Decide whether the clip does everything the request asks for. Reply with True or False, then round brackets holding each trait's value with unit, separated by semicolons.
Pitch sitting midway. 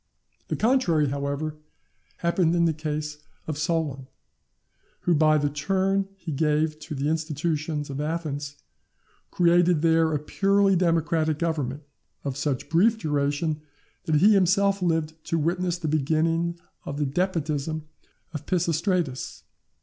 True (160 Hz)